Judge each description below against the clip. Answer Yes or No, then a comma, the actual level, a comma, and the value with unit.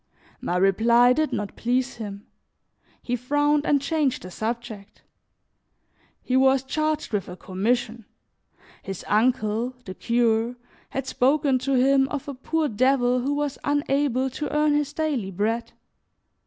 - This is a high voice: Yes, very high, 250 Hz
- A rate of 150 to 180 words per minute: No, average, 140 wpm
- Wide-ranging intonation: No, average, 4.0 semitones